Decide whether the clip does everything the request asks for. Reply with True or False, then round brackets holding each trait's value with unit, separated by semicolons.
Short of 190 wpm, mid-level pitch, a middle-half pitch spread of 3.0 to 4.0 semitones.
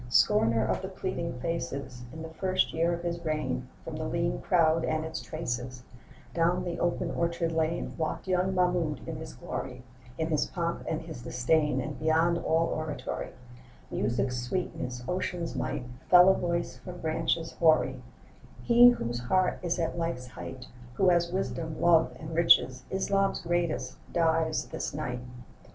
False (160 wpm; 160 Hz; 4.5 semitones)